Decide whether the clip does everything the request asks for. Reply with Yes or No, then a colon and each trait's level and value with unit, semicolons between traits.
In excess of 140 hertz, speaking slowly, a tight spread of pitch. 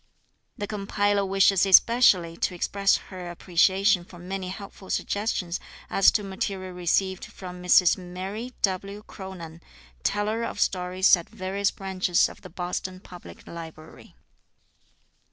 Yes: high, 190 Hz; slow, 125 wpm; narrow, 1.9 semitones